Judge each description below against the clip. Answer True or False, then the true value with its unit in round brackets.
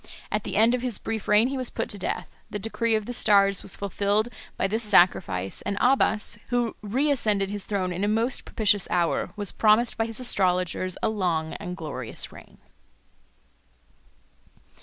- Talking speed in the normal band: True (175 wpm)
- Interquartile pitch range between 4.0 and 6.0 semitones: False (3.2 semitones)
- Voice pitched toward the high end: True (210 Hz)